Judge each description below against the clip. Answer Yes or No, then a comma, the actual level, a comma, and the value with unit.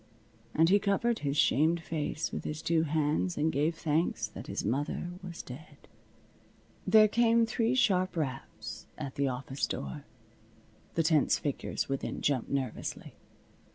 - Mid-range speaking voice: Yes, medium, 160 Hz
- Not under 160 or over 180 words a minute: No, average, 145 wpm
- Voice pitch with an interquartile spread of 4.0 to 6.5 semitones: Yes, average, 4.3 semitones